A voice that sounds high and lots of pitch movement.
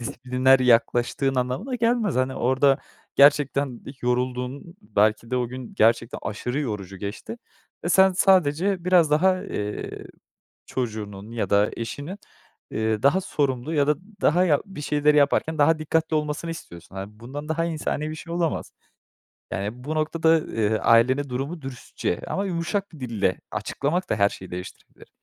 No: medium, 140 Hz; wide, 5.8 semitones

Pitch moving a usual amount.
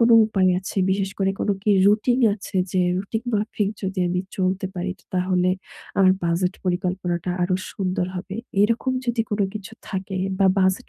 No: narrow, 2.0 semitones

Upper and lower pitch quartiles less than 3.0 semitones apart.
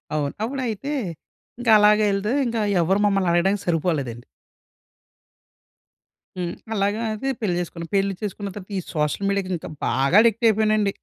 No: average, 3.7 semitones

